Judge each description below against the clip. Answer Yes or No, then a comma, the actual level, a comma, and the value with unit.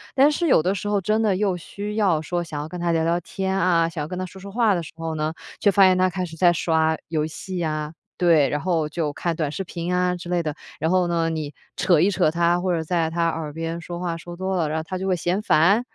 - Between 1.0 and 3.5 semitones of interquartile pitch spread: Yes, narrow, 2.5 semitones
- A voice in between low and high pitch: Yes, medium, 175 Hz